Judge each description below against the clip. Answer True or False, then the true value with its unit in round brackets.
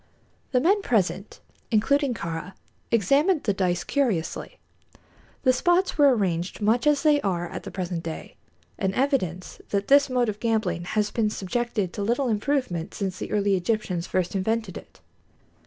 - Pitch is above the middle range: True (215 Hz)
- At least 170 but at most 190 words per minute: False (155 wpm)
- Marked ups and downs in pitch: True (5.8 semitones)